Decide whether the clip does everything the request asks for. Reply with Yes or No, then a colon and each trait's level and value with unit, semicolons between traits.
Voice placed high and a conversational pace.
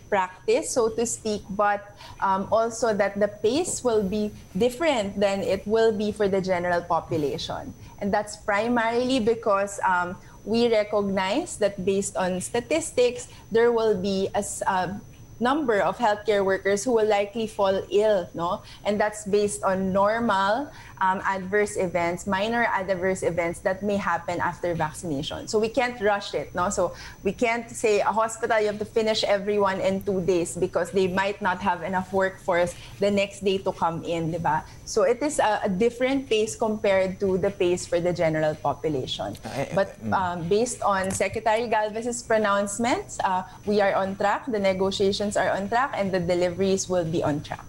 Yes: high, 200 Hz; average, 170 wpm